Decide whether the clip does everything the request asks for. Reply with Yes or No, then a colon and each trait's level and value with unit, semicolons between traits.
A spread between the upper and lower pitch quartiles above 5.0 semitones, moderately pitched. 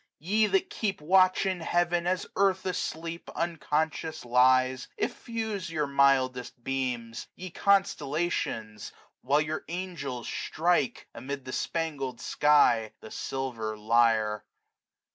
Yes: wide, 5.6 semitones; medium, 150 Hz